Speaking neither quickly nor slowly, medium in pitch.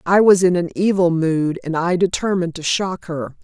No: fast, 210 wpm; medium, 175 Hz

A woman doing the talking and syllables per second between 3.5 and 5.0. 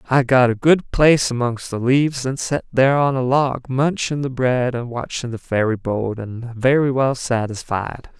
No: male; 4.6 syllables/s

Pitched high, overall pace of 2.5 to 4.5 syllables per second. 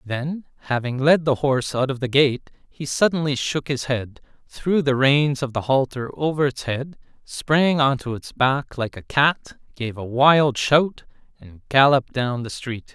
No: low, 135 Hz; 4.2 syllables/s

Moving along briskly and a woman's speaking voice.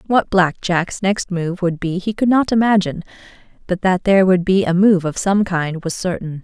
Yes: fast, 215 wpm; female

